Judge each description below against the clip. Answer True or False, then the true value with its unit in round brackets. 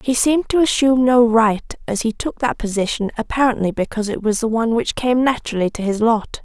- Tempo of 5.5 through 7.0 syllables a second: True (6.0 syllables/s)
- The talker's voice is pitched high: True (230 Hz)